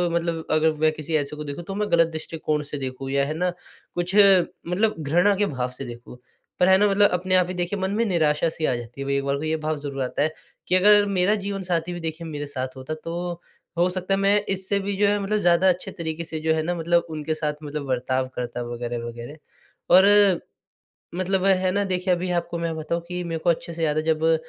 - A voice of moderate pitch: Yes, medium, 165 Hz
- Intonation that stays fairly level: No, average, 3.7 semitones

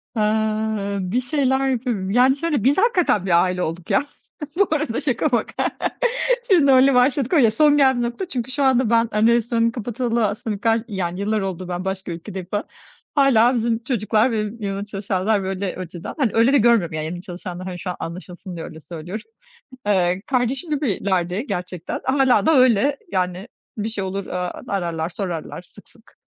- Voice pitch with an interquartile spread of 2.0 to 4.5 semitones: No, wide, 5.4 semitones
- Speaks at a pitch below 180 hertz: No, high, 215 Hz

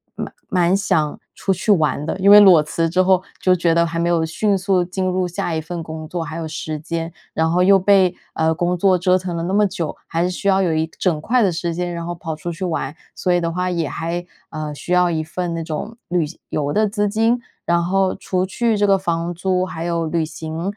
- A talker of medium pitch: Yes, medium, 175 Hz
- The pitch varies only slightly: Yes, narrow, 2.3 semitones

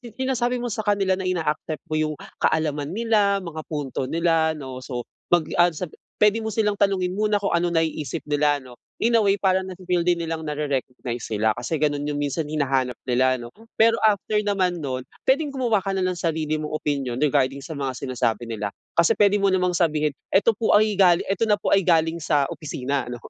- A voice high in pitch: No, medium, 165 Hz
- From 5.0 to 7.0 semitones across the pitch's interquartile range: Yes, wide, 5.6 semitones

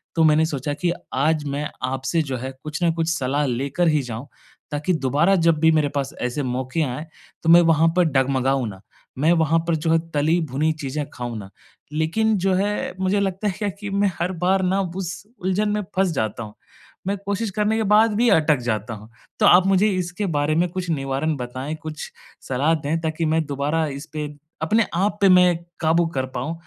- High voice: No, medium, 160 Hz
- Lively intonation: No, average, 4.6 semitones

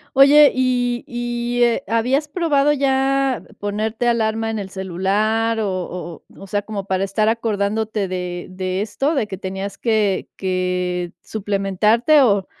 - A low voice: No, high, 215 Hz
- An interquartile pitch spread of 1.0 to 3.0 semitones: No, average, 4.0 semitones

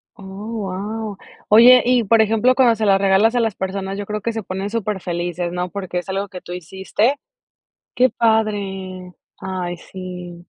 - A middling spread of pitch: Yes, average, 3.1 semitones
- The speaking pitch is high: Yes, high, 195 Hz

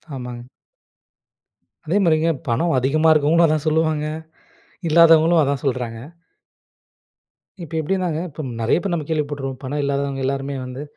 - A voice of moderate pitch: Yes, medium, 150 Hz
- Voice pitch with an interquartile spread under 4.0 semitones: Yes, average, 3.1 semitones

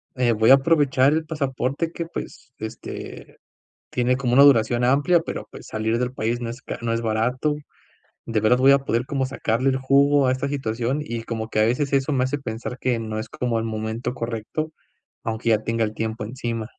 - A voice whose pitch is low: Yes, low, 125 Hz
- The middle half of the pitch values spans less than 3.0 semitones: No, average, 3.3 semitones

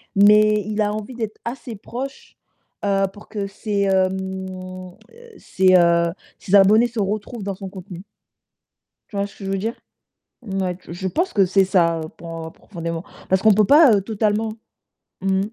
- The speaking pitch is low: No, high, 195 Hz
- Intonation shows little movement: Yes, narrow, 2.3 semitones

